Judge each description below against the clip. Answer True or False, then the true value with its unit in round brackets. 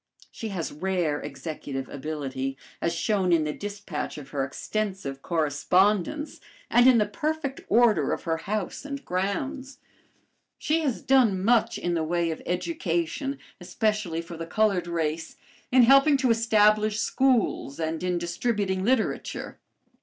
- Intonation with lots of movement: True (5.8 semitones)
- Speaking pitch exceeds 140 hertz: True (190 Hz)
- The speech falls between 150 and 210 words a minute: False (140 wpm)